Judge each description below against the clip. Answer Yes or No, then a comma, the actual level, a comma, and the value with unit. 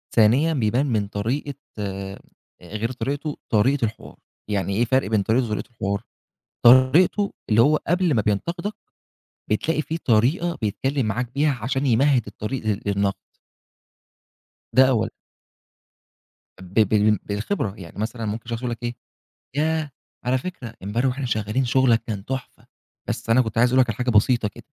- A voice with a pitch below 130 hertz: Yes, low, 120 Hz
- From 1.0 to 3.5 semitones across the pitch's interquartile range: No, average, 4.0 semitones